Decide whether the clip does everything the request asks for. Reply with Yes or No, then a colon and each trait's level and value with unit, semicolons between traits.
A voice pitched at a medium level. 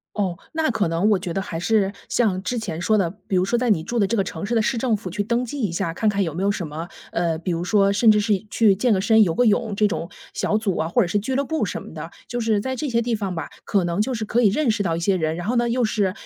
No: high, 205 Hz